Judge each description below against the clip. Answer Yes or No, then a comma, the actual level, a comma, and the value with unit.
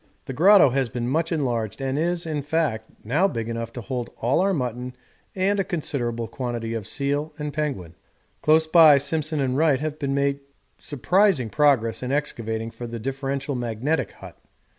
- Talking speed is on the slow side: No, average, 170 wpm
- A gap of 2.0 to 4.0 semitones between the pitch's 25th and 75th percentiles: No, average, 4.6 semitones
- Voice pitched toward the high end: No, medium, 140 Hz